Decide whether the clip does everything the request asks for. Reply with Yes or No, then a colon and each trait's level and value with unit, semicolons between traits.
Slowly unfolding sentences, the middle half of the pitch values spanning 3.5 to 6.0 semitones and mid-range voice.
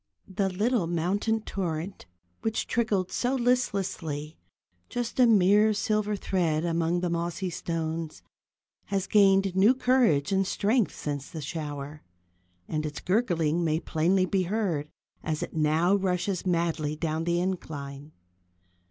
Yes: slow, 130 wpm; average, 4.2 semitones; medium, 180 Hz